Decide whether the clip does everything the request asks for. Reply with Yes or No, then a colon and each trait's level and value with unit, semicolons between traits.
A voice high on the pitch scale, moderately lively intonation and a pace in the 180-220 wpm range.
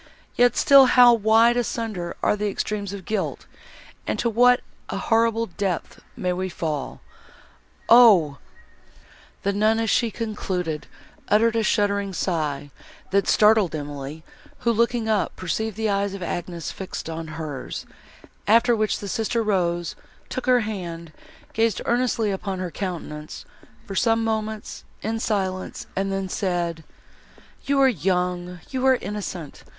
No: high, 200 Hz; average, 4.2 semitones; average, 140 wpm